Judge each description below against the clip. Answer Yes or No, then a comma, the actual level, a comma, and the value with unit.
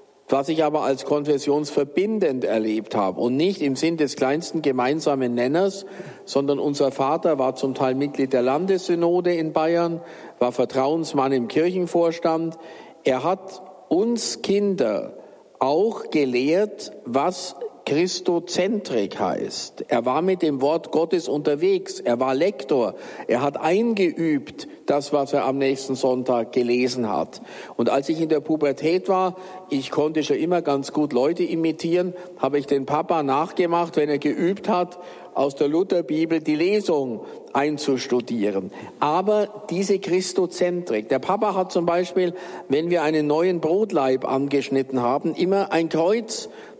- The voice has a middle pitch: Yes, medium, 160 Hz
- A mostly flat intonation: No, average, 4.8 semitones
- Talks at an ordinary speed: Yes, average, 140 wpm